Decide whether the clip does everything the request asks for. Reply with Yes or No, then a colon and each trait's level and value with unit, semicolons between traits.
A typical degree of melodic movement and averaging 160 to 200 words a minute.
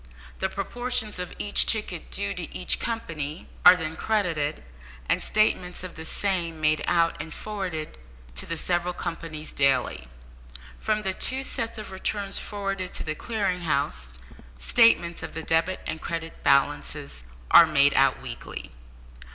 No: average, 4.4 semitones; average, 150 wpm